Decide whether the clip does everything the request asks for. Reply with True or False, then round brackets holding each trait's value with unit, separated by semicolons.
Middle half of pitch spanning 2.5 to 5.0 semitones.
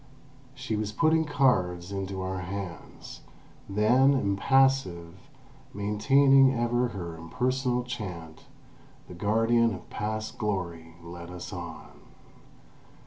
False (5.6 semitones)